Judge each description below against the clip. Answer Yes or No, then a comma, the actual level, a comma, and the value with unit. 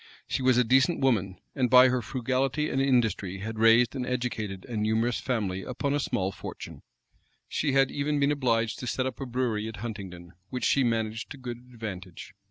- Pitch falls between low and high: No, low, 120 Hz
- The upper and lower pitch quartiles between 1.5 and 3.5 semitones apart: Yes, average, 3.2 semitones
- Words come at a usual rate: Yes, average, 190 wpm